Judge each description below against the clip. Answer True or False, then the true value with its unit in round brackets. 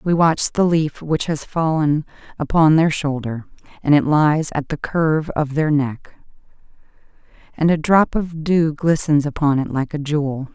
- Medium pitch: True (155 Hz)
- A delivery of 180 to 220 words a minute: False (170 wpm)